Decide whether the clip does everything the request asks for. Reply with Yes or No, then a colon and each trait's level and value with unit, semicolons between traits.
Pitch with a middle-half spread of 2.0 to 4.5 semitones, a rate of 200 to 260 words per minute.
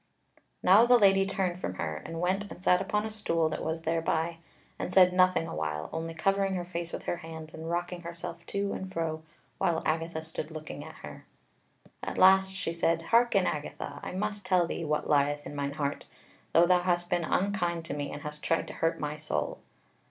Yes: average, 2.8 semitones; fast, 205 wpm